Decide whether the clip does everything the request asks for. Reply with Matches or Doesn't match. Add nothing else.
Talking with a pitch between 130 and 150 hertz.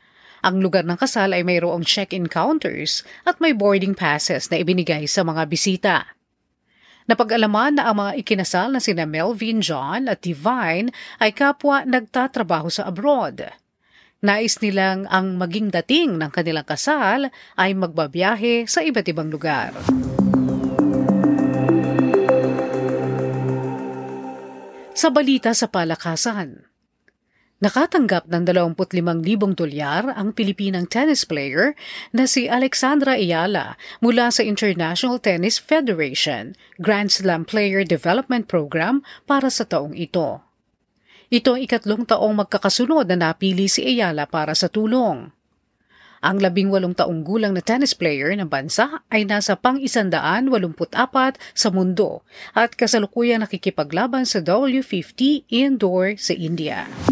Doesn't match